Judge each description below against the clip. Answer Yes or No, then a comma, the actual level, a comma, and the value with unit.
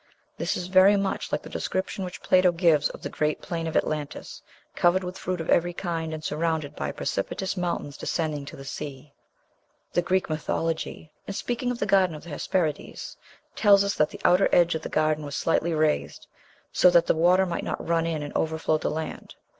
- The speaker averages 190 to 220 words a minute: Yes, average, 200 wpm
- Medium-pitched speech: Yes, medium, 165 Hz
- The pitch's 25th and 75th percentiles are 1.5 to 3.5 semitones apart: Yes, average, 2.9 semitones